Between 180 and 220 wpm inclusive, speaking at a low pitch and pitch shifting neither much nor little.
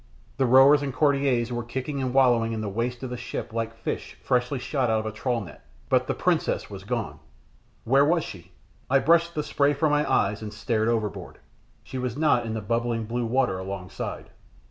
Yes: fast, 205 wpm; low, 120 Hz; average, 3.4 semitones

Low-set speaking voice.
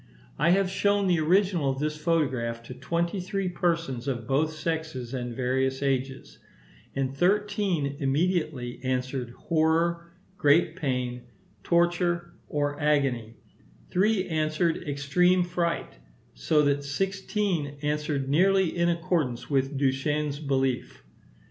No: medium, 150 Hz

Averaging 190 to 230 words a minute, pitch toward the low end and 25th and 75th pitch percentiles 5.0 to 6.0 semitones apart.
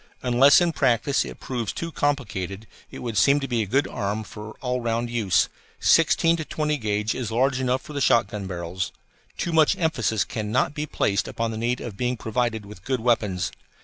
No: average, 195 wpm; low, 120 Hz; average, 4.4 semitones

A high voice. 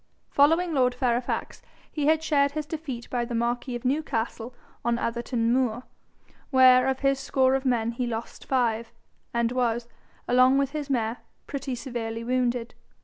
Yes: very high, 250 Hz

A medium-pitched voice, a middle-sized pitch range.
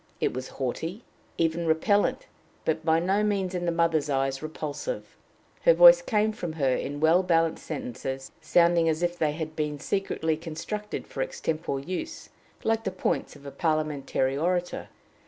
Yes: medium, 165 Hz; average, 4.0 semitones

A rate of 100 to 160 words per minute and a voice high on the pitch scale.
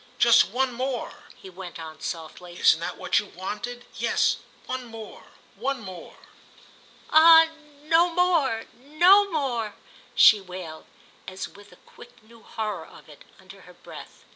Yes: average, 140 wpm; high, 225 Hz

